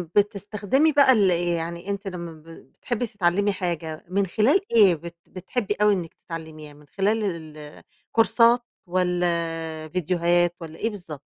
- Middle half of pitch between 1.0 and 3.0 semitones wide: No, average, 3.9 semitones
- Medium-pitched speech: Yes, medium, 180 Hz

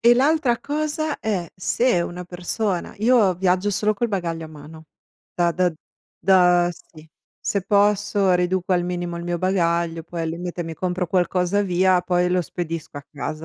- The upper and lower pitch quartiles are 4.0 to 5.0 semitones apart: No, average, 2.7 semitones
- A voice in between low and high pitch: Yes, medium, 180 Hz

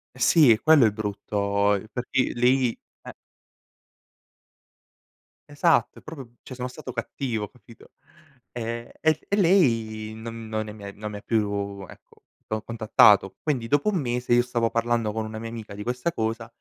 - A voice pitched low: Yes, low, 115 Hz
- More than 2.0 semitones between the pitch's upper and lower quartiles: Yes, average, 2.7 semitones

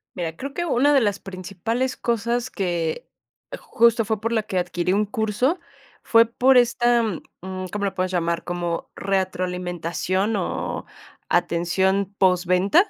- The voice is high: Yes, high, 195 Hz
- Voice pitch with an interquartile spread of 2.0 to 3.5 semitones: No, average, 4.4 semitones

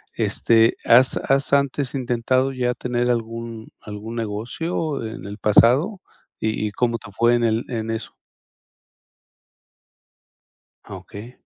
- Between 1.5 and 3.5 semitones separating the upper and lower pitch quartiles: Yes, narrow, 2.4 semitones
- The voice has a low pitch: Yes, low, 120 Hz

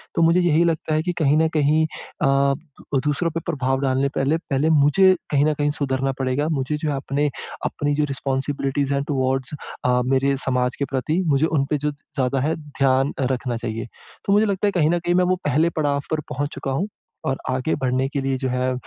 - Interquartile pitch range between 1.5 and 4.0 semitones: Yes, average, 2.7 semitones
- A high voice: No, medium, 140 Hz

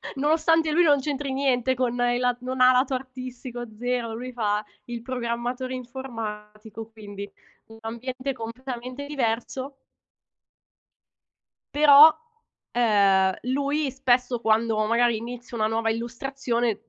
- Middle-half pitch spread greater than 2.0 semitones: Yes, narrow, 2.6 semitones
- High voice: Yes, high, 245 Hz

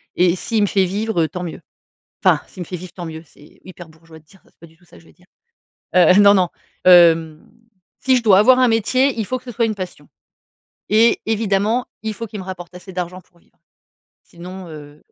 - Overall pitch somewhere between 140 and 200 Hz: Yes, medium, 185 Hz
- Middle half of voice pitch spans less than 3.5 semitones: No, average, 4.1 semitones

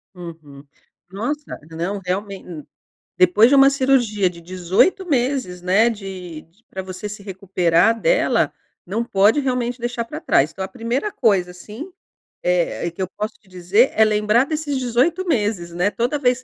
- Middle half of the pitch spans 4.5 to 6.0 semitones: Yes, wide, 5.6 semitones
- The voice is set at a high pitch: Yes, high, 210 Hz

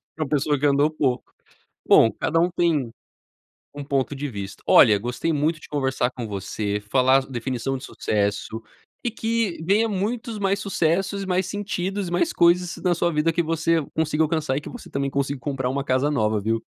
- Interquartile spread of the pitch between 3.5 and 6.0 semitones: Yes, average, 5.2 semitones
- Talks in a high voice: No, medium, 150 Hz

